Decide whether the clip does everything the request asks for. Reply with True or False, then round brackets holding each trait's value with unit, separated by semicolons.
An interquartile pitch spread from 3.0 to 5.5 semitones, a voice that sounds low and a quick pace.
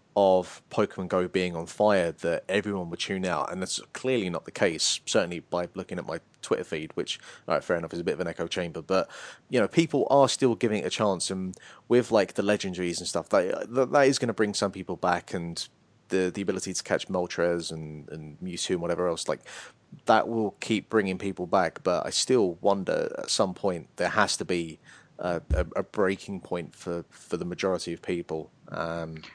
True (3.5 semitones; 95 Hz; 215 wpm)